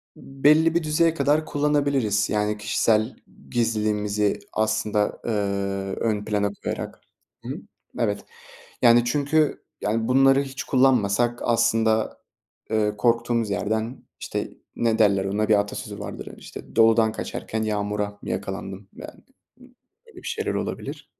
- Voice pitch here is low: Yes, low, 110 Hz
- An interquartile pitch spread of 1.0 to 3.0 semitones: No, average, 4.2 semitones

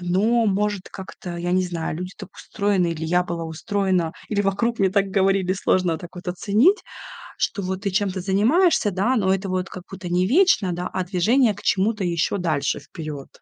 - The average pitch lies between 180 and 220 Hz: Yes, high, 190 Hz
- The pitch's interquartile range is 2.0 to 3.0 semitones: Yes, narrow, 2.4 semitones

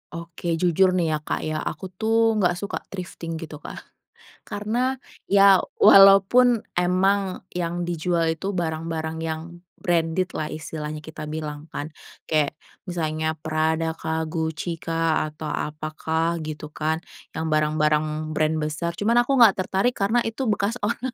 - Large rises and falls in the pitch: No, average, 3.5 semitones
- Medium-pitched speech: Yes, medium, 165 Hz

